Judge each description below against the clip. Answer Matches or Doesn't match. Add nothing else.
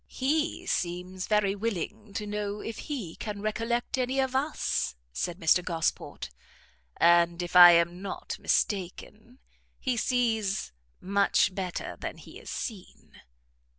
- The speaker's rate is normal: Doesn't match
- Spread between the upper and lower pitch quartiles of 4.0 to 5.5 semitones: Matches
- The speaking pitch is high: Matches